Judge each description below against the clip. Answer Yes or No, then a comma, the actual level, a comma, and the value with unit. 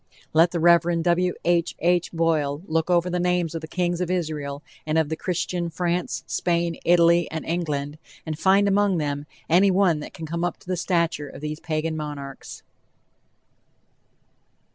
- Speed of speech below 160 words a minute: No, average, 165 wpm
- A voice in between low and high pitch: Yes, medium, 170 Hz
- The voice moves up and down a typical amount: No, narrow, 2.2 semitones